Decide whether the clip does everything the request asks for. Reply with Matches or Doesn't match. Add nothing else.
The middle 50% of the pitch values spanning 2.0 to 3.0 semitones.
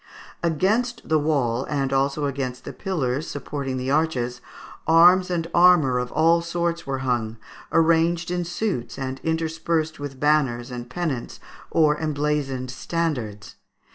Doesn't match